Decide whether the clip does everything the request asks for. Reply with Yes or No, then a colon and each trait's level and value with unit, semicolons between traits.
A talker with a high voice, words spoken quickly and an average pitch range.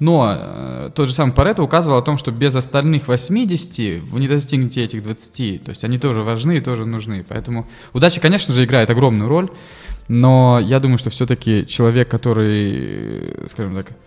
No: low, 125 Hz; fast, 175 wpm; average, 4.7 semitones